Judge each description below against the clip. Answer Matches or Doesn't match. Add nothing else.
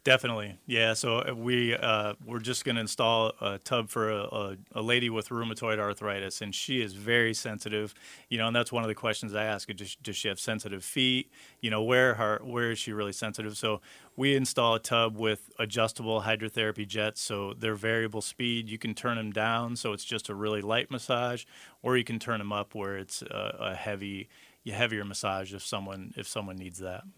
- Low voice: Matches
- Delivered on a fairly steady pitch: Matches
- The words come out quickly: Matches